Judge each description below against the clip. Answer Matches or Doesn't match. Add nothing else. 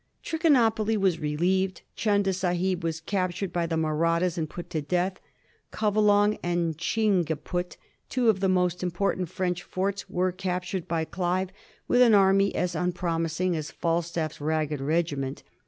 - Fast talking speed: Doesn't match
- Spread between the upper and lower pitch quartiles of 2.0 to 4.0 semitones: Matches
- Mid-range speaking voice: Matches